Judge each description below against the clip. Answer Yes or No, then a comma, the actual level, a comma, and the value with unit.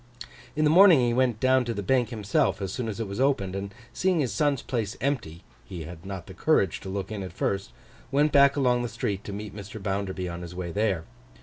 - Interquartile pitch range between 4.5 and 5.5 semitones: Yes, average, 5.1 semitones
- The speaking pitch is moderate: No, low, 105 Hz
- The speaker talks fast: Yes, fast, 235 wpm